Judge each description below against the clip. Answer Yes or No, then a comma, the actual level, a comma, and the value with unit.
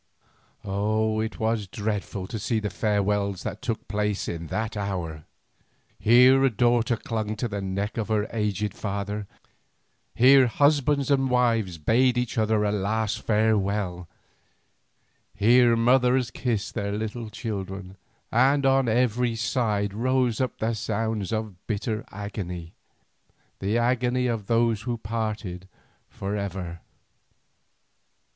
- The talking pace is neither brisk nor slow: No, slow, 125 wpm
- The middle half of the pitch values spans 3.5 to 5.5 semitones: No, average, 2.8 semitones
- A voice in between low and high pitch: No, low, 110 Hz